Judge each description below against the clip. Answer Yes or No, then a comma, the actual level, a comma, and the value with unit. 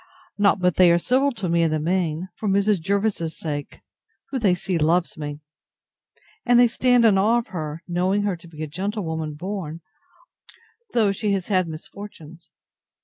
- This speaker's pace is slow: No, average, 175 wpm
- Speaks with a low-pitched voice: No, medium, 185 Hz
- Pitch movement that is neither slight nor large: Yes, average, 4.0 semitones